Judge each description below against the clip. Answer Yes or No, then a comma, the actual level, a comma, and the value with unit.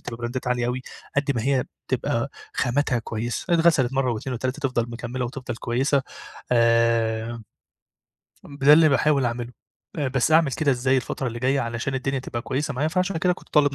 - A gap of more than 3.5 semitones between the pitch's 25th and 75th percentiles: No, average, 3.1 semitones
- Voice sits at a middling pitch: No, low, 130 Hz